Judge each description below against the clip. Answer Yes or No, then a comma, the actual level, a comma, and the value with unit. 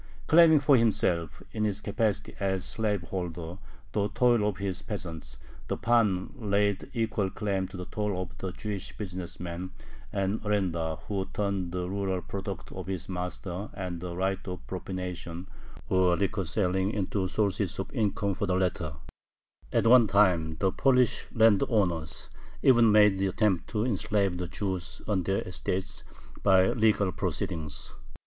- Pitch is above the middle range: No, very low, 95 Hz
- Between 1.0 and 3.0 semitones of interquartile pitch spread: Yes, narrow, 2.5 semitones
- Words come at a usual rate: Yes, average, 150 wpm